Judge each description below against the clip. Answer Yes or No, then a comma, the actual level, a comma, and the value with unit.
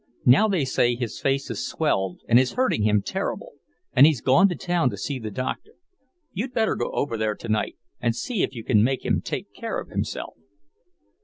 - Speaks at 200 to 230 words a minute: Yes, fast, 205 wpm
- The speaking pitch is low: Yes, low, 130 Hz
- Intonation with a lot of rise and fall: Yes, wide, 7.1 semitones